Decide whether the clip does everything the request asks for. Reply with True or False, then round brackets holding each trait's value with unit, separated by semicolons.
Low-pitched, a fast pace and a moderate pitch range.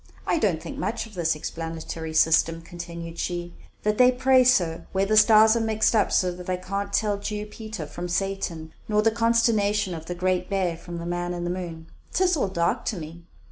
False (185 Hz; 210 wpm; 4.0 semitones)